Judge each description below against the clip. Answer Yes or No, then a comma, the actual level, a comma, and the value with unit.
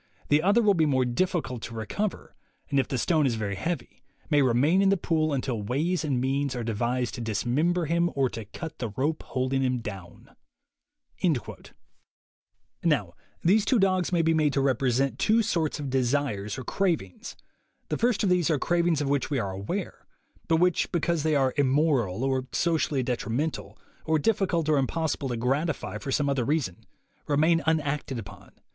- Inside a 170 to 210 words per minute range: Yes, average, 180 wpm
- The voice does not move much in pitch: No, average, 4.9 semitones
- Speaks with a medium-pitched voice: Yes, medium, 145 Hz